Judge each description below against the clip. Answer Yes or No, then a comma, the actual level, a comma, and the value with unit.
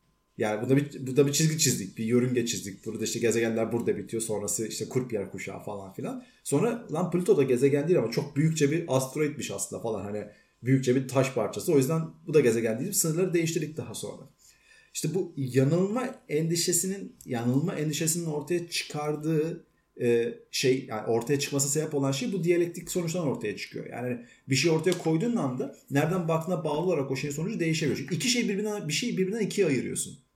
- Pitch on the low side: No, medium, 145 Hz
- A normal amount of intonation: No, wide, 5.8 semitones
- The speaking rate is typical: No, fast, 190 wpm